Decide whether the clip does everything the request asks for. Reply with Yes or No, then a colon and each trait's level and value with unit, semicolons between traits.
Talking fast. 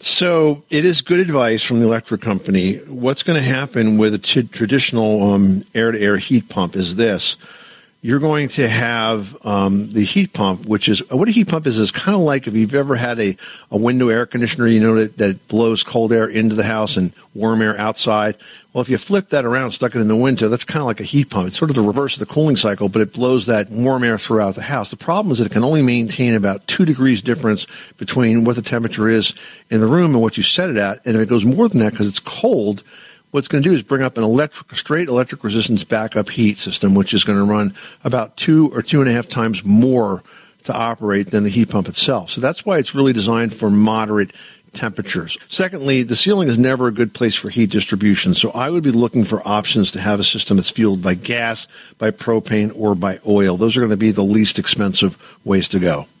Yes: fast, 240 wpm